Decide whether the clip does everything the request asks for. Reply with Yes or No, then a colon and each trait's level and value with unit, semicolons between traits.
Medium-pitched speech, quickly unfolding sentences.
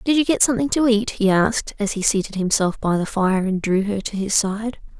No: high, 210 Hz; fast, 250 wpm